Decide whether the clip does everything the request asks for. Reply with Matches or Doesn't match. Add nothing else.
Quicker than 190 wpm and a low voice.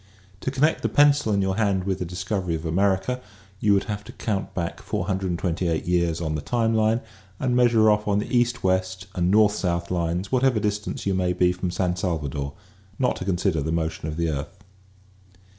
Matches